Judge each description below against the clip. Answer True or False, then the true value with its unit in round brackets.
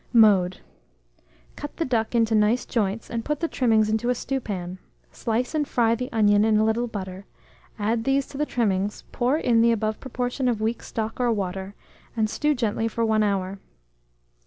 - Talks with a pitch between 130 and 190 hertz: False (225 Hz)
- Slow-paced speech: False (185 wpm)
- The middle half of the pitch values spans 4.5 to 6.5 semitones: False (2.8 semitones)